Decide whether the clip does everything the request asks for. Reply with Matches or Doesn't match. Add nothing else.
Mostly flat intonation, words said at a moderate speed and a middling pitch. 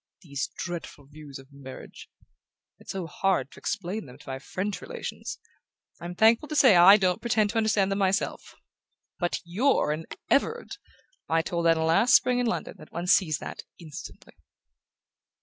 Doesn't match